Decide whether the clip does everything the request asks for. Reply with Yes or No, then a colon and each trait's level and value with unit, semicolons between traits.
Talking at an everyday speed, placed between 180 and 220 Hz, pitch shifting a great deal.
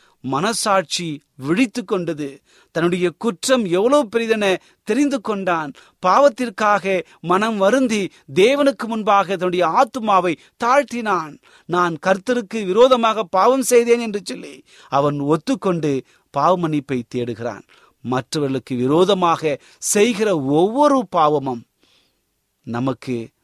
Yes: average, 85 wpm; high, 190 Hz; wide, 7.2 semitones